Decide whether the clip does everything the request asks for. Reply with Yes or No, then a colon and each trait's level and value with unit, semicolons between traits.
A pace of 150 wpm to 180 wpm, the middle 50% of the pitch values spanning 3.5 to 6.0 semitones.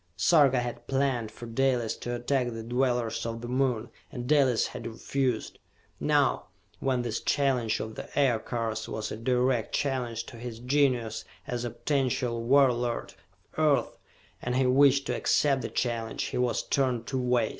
No: average, 165 wpm; narrow, 2.5 semitones